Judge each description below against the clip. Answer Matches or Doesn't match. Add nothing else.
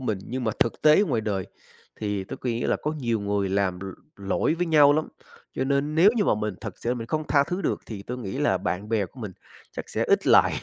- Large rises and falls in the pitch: Matches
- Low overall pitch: Matches